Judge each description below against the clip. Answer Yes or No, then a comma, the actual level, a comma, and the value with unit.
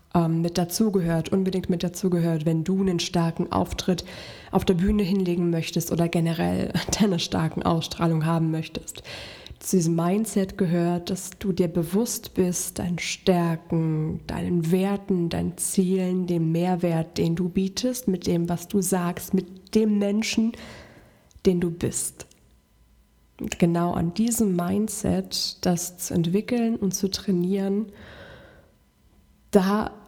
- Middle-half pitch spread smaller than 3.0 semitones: Yes, narrow, 2.4 semitones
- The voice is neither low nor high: Yes, medium, 180 Hz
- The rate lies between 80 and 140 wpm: Yes, average, 130 wpm